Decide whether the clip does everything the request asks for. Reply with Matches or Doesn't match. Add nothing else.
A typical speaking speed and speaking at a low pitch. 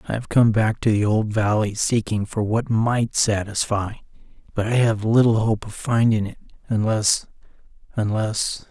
Matches